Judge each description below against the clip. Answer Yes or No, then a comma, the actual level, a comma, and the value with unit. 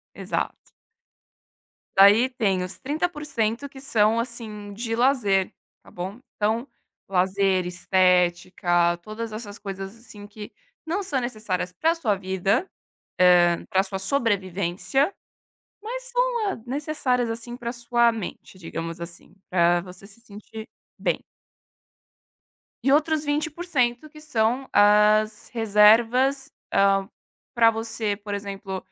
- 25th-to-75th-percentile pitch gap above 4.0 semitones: Yes, average, 4.8 semitones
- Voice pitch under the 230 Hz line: Yes, high, 215 Hz